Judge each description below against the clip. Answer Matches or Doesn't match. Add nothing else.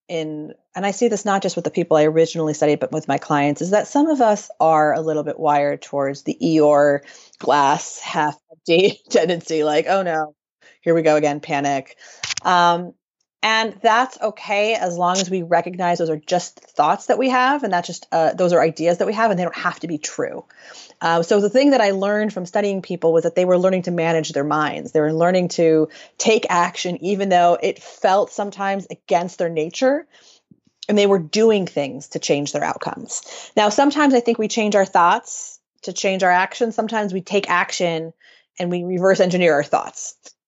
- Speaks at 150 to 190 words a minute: Doesn't match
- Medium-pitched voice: Matches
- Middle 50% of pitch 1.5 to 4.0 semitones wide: Doesn't match